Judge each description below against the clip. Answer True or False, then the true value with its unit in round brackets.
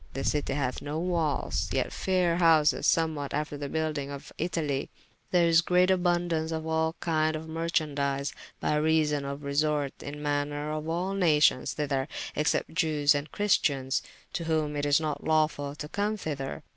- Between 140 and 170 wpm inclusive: True (165 wpm)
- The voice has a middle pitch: True (155 Hz)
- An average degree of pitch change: False (2.2 semitones)